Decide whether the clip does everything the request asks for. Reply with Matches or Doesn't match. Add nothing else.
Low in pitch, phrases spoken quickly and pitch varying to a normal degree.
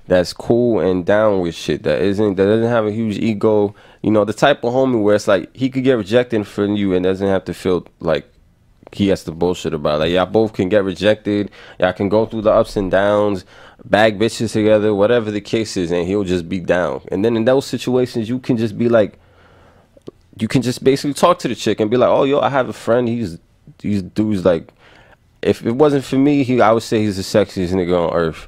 Matches